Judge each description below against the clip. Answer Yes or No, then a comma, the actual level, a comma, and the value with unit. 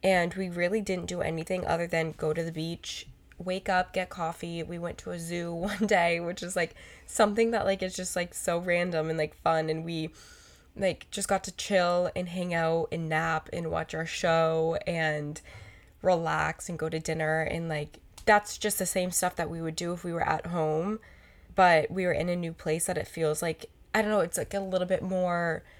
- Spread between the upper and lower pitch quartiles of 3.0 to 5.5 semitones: No, narrow, 2.4 semitones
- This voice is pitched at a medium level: Yes, medium, 170 Hz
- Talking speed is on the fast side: Yes, fast, 220 wpm